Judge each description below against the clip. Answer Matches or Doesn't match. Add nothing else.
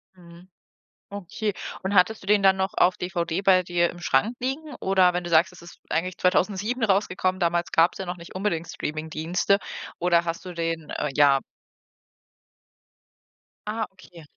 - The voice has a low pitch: Doesn't match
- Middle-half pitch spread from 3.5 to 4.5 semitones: Doesn't match